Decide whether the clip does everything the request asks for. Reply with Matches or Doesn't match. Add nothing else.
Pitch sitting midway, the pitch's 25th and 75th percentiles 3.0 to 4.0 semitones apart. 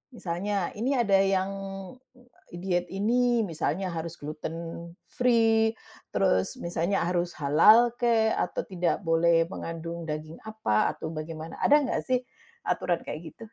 Doesn't match